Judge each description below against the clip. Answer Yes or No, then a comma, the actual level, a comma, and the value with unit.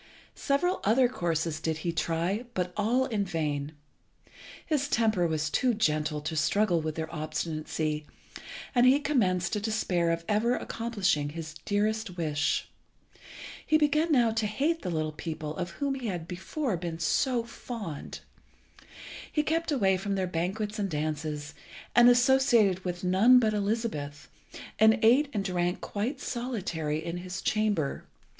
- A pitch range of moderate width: No, wide, 6.5 semitones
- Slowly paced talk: No, average, 150 wpm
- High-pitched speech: Yes, high, 195 Hz